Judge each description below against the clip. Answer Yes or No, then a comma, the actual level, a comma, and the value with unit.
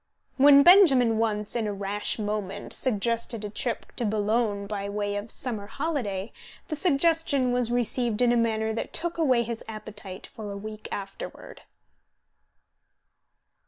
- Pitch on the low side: No, high, 225 Hz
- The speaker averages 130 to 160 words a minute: Yes, average, 145 wpm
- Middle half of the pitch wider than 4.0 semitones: No, average, 3.3 semitones